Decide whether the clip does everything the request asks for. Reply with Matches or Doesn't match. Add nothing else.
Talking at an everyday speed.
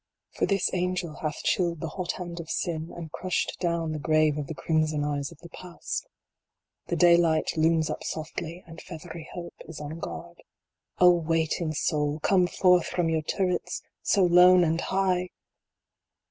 Matches